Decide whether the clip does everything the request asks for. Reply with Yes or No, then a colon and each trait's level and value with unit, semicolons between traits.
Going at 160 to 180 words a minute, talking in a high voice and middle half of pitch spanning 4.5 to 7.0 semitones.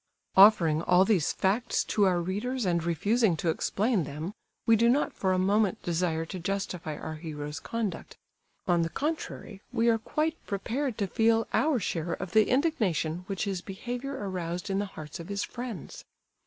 Yes: average, 175 wpm; high, 195 Hz; average, 4.9 semitones